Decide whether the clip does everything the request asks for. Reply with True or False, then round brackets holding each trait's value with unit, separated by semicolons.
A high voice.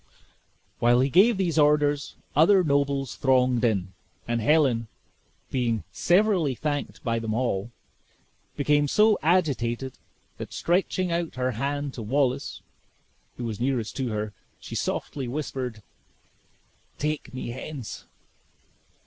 False (135 Hz)